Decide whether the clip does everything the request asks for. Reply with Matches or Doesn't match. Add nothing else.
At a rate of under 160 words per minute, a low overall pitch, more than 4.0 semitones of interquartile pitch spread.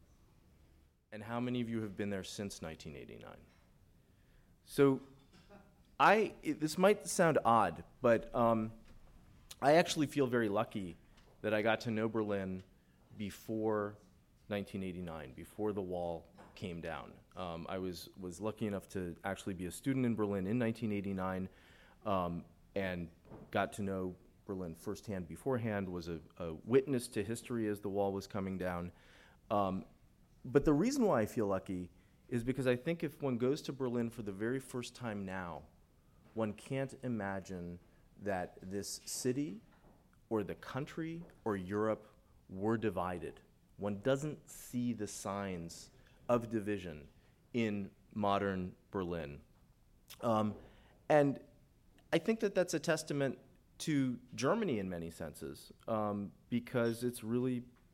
Matches